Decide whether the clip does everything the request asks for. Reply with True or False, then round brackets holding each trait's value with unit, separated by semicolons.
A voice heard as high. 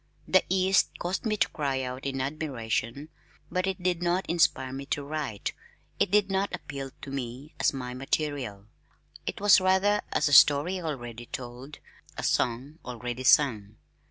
False (140 Hz)